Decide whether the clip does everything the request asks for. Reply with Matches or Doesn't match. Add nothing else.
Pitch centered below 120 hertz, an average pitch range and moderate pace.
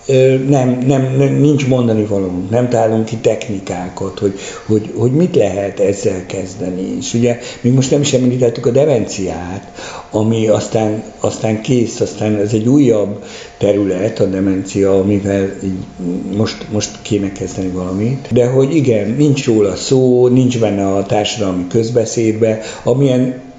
Matches